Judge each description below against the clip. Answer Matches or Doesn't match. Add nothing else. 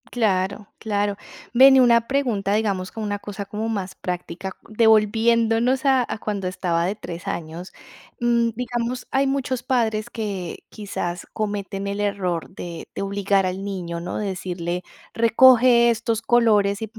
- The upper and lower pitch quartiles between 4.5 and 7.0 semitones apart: Doesn't match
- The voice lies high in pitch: Matches